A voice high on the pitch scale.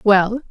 Yes: high, 215 Hz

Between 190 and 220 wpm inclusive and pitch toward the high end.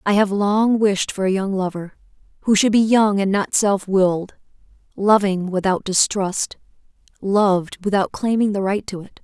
No: average, 170 wpm; high, 200 Hz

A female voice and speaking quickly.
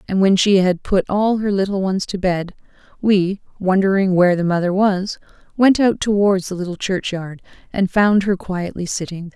No: female; average, 180 wpm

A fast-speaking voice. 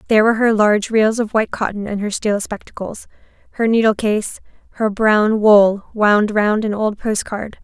No: average, 180 wpm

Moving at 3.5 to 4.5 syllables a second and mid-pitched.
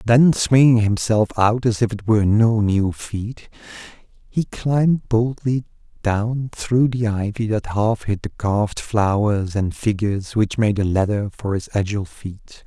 No: 4.2 syllables/s; low, 110 Hz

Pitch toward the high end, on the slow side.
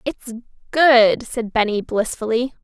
Yes: high, 235 Hz; slow, 115 wpm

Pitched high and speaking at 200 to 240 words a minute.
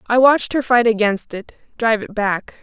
Yes: high, 225 Hz; fast, 205 wpm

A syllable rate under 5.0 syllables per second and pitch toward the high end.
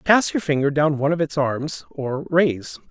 No: 4.5 syllables/s; medium, 150 Hz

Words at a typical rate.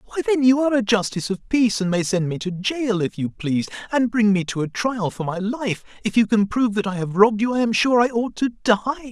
No: fast, 275 wpm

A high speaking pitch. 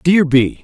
No: medium, 155 Hz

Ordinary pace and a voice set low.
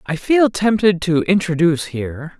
No: average, 150 wpm; medium, 180 Hz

